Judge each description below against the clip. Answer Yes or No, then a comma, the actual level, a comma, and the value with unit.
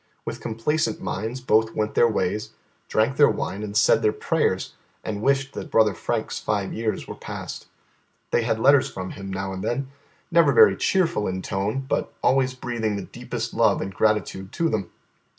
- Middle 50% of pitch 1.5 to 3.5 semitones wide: No, average, 4.6 semitones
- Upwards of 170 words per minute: Yes, average, 180 wpm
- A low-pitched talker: Yes, low, 110 Hz